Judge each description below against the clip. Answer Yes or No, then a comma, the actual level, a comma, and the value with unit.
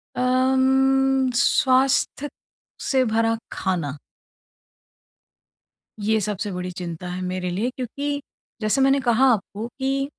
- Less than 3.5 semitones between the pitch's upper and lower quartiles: No, wide, 5.6 semitones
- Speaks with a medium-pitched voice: No, high, 245 Hz